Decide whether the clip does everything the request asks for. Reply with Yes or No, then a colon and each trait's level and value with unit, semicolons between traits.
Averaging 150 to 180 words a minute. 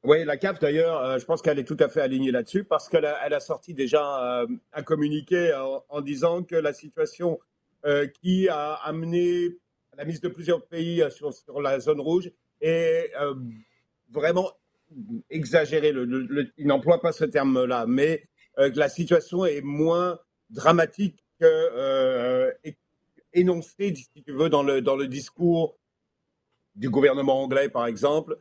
Yes: average, 165 wpm